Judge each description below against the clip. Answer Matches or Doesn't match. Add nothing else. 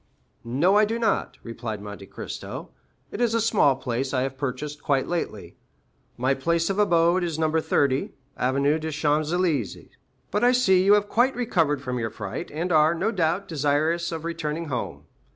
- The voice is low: Doesn't match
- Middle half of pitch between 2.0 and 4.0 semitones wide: Doesn't match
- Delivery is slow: Doesn't match